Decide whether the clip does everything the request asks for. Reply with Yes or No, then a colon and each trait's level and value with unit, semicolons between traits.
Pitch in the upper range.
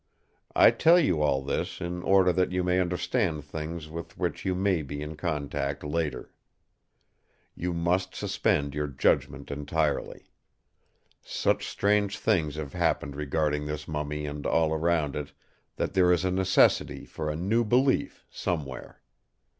No: very low, 80 Hz